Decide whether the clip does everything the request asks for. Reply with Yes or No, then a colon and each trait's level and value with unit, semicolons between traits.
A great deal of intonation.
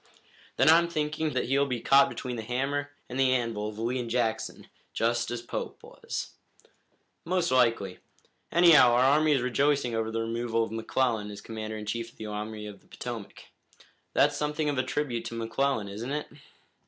No: average, 3.8 semitones